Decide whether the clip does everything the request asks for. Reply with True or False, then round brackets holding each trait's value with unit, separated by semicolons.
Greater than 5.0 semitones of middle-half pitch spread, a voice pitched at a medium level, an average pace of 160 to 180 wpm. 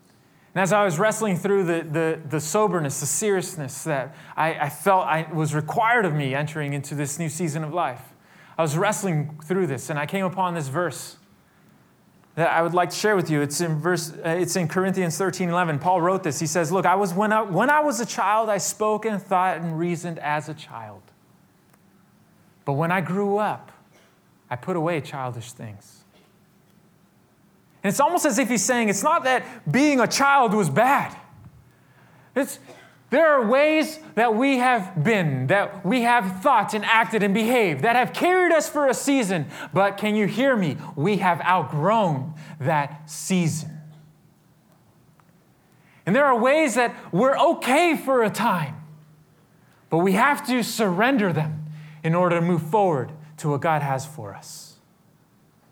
True (5.4 semitones; 180 Hz; 175 wpm)